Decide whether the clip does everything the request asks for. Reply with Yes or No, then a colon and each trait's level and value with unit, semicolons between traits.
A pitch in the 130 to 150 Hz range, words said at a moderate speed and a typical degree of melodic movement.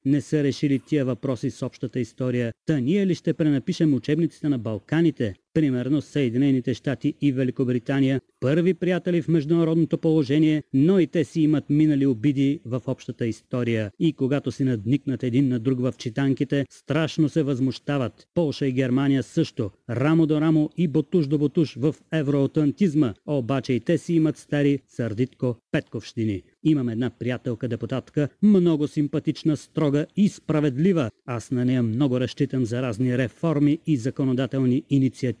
Yes: medium, 140 Hz; average, 150 wpm; average, 3.4 semitones